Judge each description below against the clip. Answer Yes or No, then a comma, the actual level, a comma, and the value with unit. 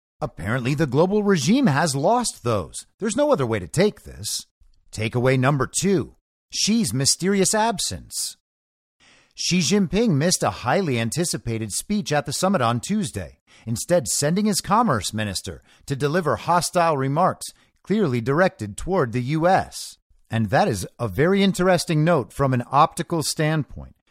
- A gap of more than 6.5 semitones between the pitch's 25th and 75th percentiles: Yes, wide, 8.9 semitones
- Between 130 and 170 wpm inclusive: Yes, average, 140 wpm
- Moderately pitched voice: Yes, medium, 145 Hz